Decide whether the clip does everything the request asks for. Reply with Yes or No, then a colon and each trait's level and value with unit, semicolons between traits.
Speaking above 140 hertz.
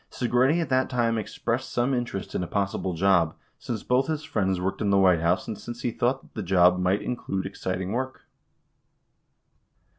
No: low, 105 Hz